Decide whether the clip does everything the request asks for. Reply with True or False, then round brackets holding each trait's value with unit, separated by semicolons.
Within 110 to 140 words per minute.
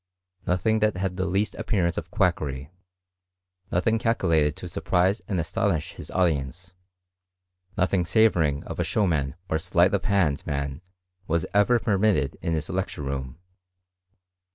True (135 wpm)